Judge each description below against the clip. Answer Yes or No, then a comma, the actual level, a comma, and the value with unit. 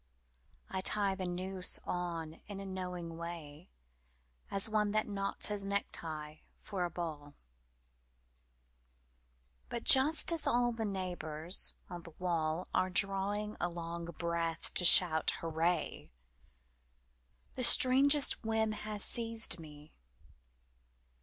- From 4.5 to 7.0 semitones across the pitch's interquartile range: No, average, 3.9 semitones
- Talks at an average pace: No, slow, 115 wpm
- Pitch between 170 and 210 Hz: Yes, medium, 185 Hz